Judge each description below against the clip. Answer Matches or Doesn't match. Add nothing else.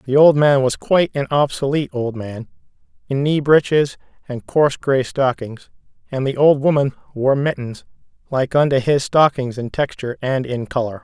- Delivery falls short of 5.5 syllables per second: Matches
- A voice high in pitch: Doesn't match